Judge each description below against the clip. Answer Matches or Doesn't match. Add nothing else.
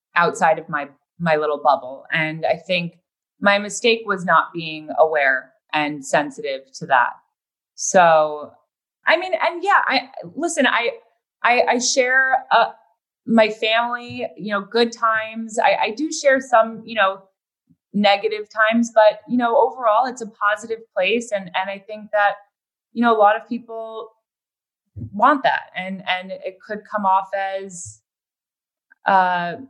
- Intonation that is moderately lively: Matches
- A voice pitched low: Doesn't match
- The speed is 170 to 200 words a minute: Doesn't match